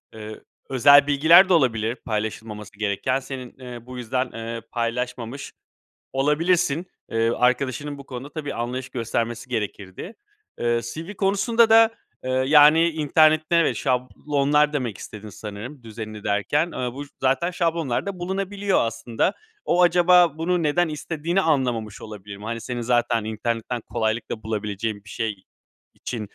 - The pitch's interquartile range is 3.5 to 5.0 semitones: No, wide, 5.6 semitones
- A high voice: No, low, 130 Hz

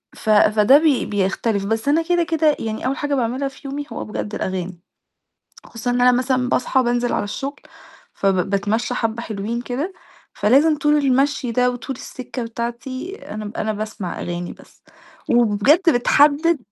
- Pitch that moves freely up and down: No, average, 4.6 semitones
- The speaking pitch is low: No, high, 245 Hz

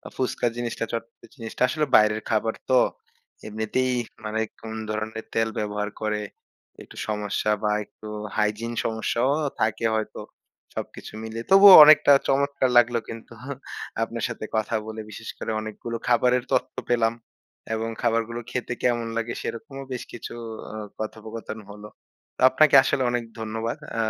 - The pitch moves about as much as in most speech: No, narrow, 2.0 semitones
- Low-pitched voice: Yes, low, 115 Hz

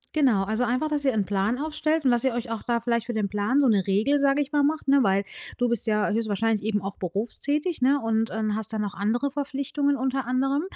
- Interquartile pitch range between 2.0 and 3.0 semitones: No, average, 4.8 semitones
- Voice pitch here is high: Yes, high, 240 Hz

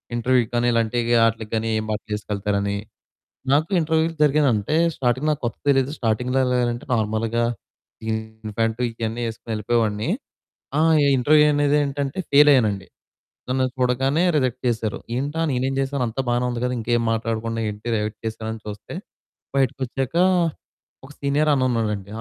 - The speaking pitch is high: No, low, 120 Hz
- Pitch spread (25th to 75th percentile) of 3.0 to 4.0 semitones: Yes, average, 3.4 semitones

